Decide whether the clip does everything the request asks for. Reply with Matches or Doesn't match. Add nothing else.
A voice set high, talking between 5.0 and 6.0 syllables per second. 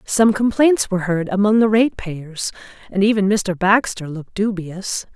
Doesn't match